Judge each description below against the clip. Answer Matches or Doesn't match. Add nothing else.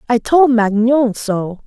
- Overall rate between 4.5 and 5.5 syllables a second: Doesn't match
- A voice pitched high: Matches